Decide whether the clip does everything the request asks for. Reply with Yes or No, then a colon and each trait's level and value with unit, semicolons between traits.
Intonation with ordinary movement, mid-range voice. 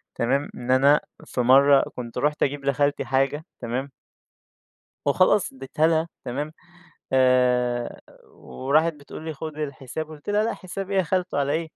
Yes: average, 3.3 semitones; medium, 145 Hz